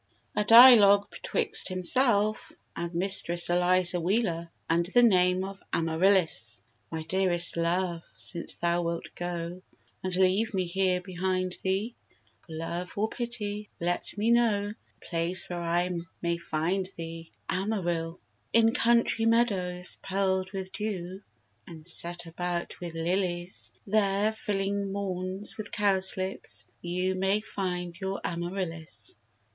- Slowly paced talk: Yes, slow, 130 wpm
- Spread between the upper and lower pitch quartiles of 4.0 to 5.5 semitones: No, narrow, 2.6 semitones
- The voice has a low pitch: No, medium, 185 Hz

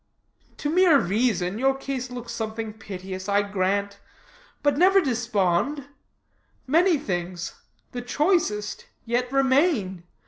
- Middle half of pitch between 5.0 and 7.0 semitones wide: Yes, wide, 5.5 semitones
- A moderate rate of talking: No, slow, 110 wpm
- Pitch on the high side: Yes, high, 235 Hz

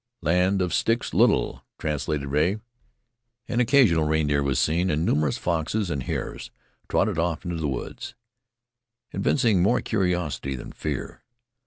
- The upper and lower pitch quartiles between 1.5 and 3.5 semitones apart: No, average, 4.1 semitones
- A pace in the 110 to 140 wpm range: Yes, slow, 135 wpm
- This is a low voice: Yes, very low, 80 Hz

